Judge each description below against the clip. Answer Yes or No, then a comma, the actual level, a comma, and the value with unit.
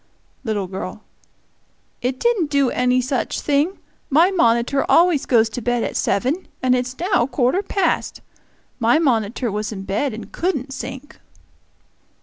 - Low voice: No, very high, 255 Hz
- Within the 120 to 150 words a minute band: Yes, average, 140 wpm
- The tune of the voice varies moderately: Yes, average, 4.2 semitones